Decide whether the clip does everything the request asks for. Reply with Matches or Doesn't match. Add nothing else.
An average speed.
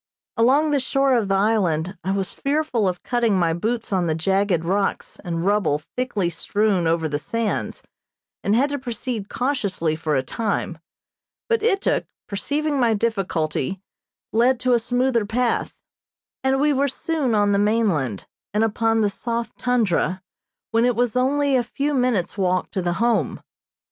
Matches